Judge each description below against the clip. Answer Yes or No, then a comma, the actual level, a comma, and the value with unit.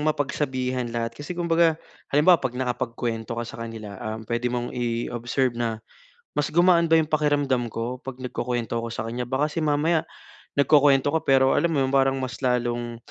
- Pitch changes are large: No, average, 3.7 semitones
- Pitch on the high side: No, low, 130 Hz